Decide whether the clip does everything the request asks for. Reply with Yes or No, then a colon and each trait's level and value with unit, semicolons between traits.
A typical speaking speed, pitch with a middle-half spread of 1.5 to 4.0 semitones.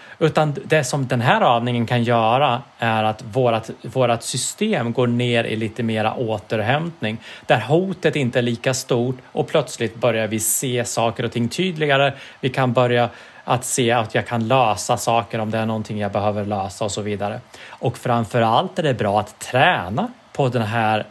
Yes: average, 180 wpm; average, 2.9 semitones